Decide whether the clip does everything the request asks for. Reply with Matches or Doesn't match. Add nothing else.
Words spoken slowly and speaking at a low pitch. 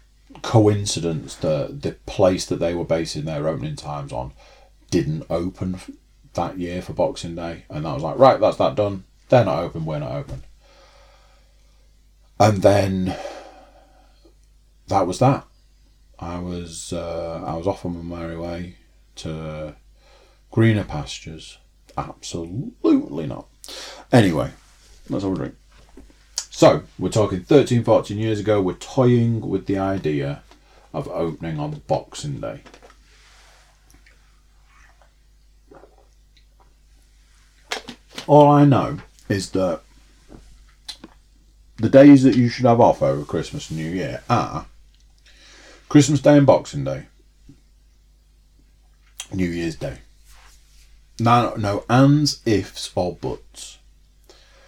Matches